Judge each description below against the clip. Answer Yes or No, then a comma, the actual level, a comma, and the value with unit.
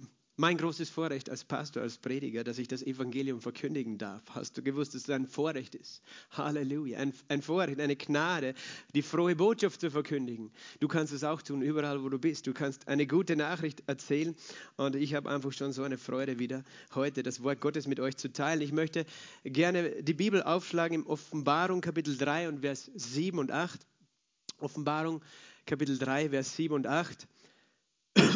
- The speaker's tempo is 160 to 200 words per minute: Yes, average, 180 wpm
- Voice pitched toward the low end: No, medium, 145 Hz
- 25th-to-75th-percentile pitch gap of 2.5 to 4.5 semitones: Yes, average, 2.9 semitones